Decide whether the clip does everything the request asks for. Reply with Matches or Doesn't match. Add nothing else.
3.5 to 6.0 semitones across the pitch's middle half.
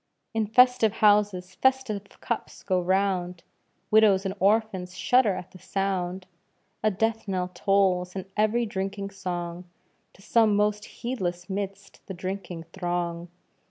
Doesn't match